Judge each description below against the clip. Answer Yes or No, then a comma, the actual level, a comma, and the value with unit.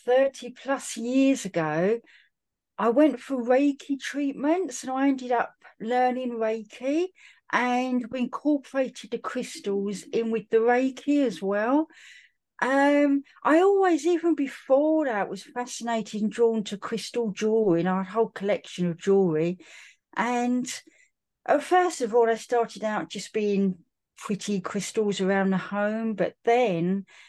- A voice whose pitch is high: Yes, high, 240 Hz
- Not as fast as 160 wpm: Yes, slow, 135 wpm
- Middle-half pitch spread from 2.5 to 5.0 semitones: Yes, average, 4.7 semitones